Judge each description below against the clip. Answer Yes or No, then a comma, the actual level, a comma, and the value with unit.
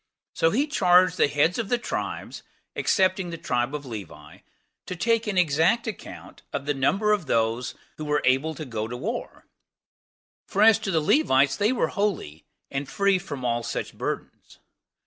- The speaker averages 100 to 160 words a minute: No, average, 175 wpm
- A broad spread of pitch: Yes, wide, 7.1 semitones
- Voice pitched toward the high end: No, medium, 165 Hz